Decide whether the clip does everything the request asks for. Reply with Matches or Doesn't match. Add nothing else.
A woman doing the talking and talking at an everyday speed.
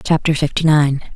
Matches